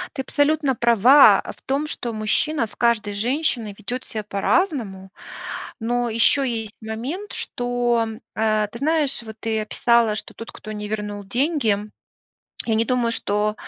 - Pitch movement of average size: Yes, average, 3.6 semitones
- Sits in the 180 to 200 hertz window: No, high, 230 Hz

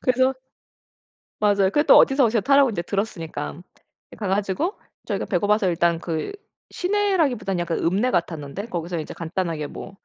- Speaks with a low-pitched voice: No, high, 195 Hz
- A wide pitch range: Yes, wide, 6.8 semitones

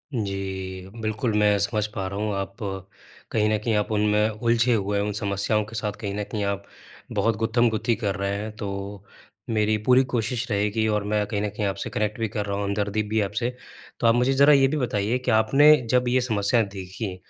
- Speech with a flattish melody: Yes, narrow, 2.3 semitones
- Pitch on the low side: Yes, low, 105 Hz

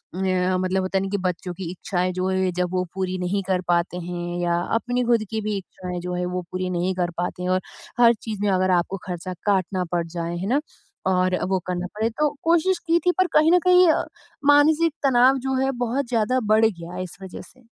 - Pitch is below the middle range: No, high, 190 Hz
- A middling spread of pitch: Yes, average, 4.7 semitones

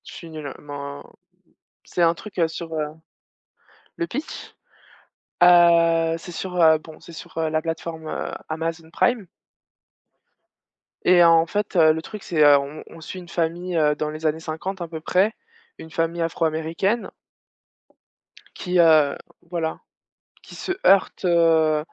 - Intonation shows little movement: Yes, narrow, 1.8 semitones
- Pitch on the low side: No, medium, 165 Hz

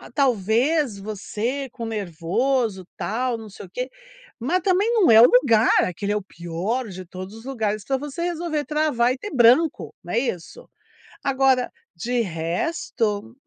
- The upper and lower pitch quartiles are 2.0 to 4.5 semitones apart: No, average, 5.0 semitones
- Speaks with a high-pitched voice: Yes, high, 235 Hz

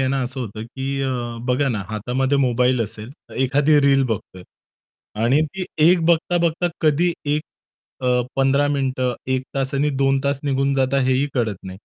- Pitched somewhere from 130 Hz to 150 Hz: Yes, low, 135 Hz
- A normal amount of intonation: No, narrow, 2.1 semitones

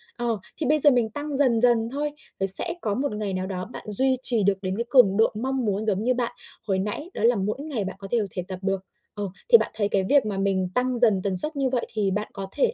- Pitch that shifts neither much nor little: Yes, average, 4.7 semitones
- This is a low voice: No, high, 220 Hz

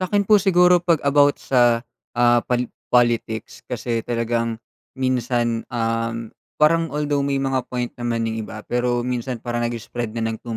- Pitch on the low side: Yes, low, 120 Hz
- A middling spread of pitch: Yes, average, 3.1 semitones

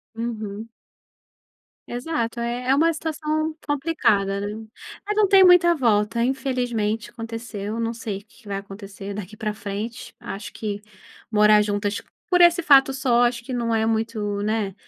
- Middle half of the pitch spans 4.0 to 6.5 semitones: Yes, average, 4.4 semitones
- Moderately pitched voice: No, high, 230 Hz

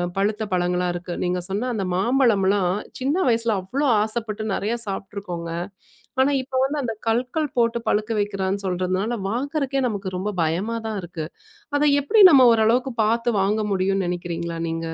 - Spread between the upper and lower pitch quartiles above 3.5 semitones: Yes, average, 4.4 semitones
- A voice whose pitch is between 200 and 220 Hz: Yes, high, 210 Hz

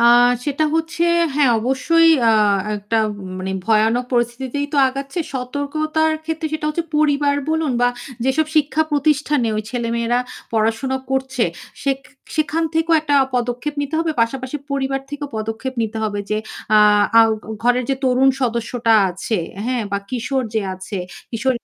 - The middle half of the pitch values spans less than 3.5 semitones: No, average, 4.1 semitones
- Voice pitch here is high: Yes, very high, 265 Hz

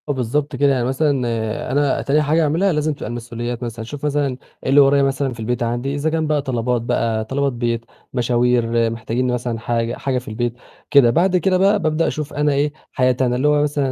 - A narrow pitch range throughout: No, average, 3.6 semitones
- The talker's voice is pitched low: Yes, low, 130 Hz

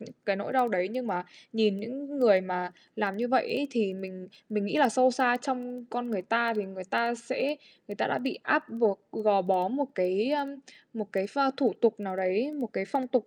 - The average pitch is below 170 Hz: No, high, 230 Hz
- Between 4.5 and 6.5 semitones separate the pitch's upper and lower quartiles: Yes, average, 4.8 semitones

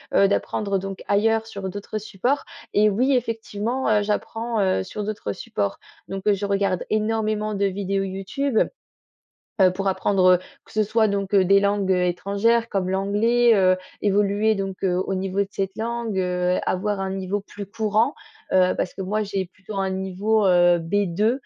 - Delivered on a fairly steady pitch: Yes, narrow, 2.1 semitones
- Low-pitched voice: No, high, 200 Hz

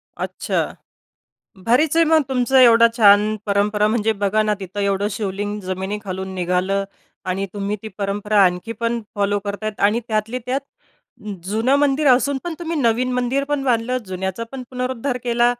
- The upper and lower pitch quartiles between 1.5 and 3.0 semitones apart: No, average, 3.9 semitones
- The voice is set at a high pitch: Yes, high, 215 Hz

